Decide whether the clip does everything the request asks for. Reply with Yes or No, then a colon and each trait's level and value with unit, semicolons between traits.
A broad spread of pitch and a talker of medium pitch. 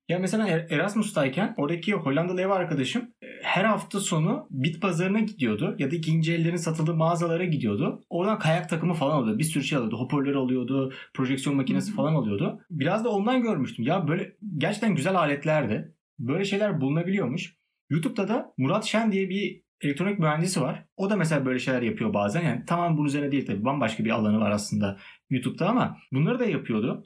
Yes: wide, 5.8 semitones; medium, 170 Hz